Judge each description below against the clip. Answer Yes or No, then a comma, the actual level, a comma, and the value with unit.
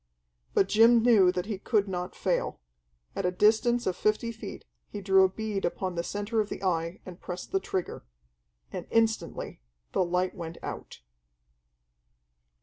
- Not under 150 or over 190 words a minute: Yes, average, 160 wpm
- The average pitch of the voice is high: Yes, high, 195 Hz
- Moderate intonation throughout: Yes, average, 3.3 semitones